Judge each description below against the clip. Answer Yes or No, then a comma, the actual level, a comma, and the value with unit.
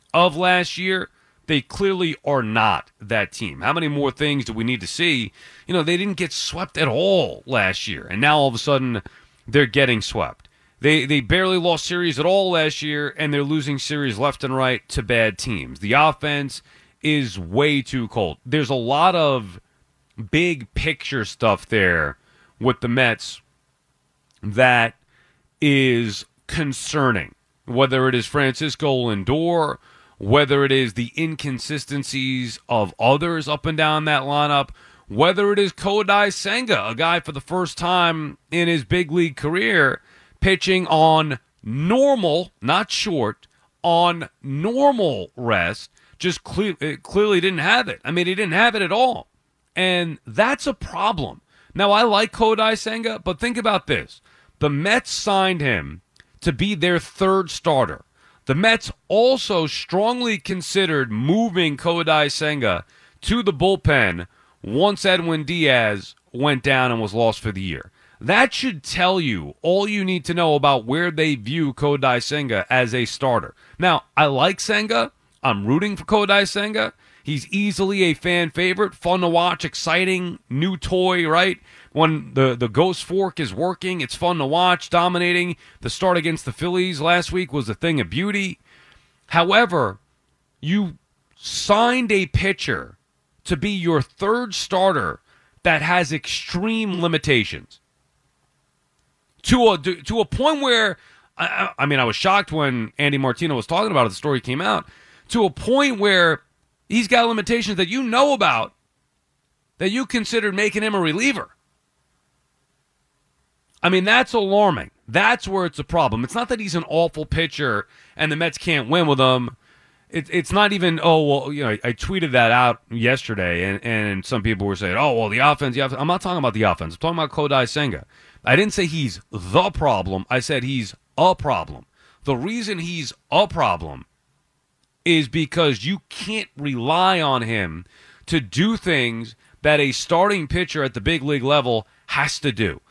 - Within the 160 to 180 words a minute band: Yes, average, 165 wpm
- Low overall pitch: No, medium, 160 Hz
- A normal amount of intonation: No, wide, 5.9 semitones